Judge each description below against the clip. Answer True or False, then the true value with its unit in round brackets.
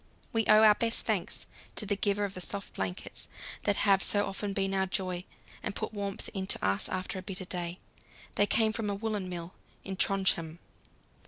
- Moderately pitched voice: False (195 Hz)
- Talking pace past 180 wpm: True (190 wpm)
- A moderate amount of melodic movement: False (1.9 semitones)